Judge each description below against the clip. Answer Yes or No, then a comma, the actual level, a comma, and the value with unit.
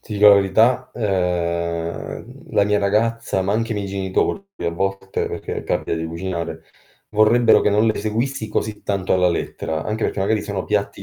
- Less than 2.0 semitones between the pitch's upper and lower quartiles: No, average, 2.8 semitones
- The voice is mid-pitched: No, low, 100 Hz